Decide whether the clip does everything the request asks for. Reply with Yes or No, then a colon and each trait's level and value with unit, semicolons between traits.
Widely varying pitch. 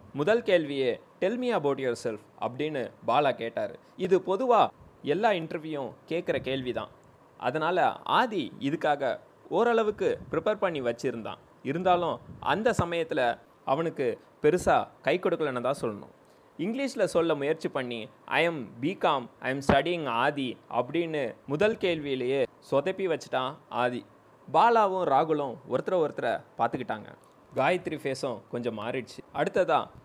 Yes: wide, 6.2 semitones